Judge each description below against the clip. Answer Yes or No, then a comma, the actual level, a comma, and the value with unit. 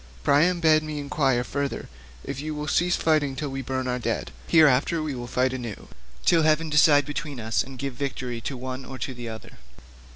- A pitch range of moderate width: Yes, average, 3.2 semitones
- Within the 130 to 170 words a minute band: No, average, 200 wpm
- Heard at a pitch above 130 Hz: Yes, medium, 140 Hz